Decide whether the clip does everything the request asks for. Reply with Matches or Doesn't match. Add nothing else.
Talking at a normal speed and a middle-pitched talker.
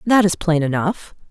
Matches